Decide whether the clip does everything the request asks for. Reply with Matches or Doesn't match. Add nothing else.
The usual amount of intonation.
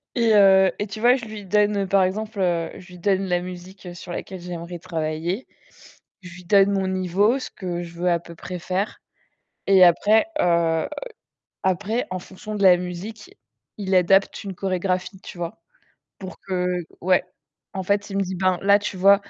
Doesn't match